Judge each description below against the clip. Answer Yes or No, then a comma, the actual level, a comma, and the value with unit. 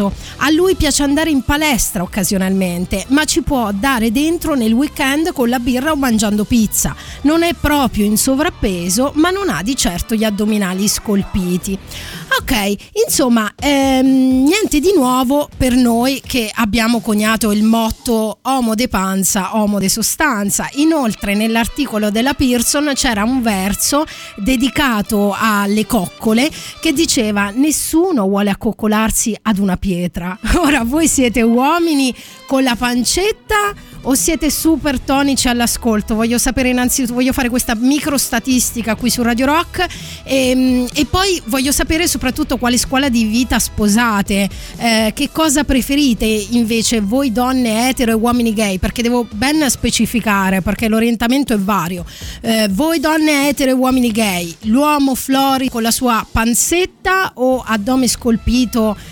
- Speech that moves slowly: No, average, 140 wpm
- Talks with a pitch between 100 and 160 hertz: No, high, 245 Hz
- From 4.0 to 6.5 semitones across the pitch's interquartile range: Yes, average, 4.3 semitones